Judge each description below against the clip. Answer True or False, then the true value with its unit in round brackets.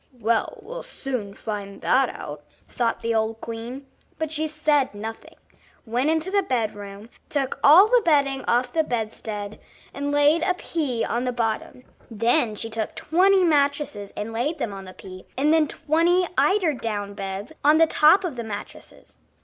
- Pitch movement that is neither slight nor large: False (6.0 semitones)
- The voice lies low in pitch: False (250 Hz)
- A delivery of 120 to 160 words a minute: False (170 wpm)